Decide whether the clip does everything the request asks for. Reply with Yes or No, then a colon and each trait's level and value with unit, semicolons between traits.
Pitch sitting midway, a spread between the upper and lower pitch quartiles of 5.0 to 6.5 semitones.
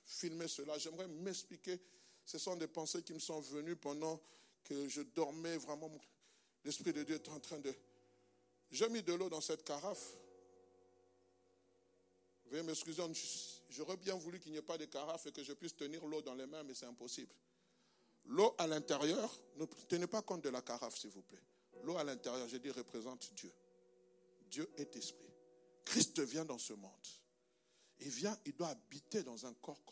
Yes: medium, 145 Hz; average, 5.3 semitones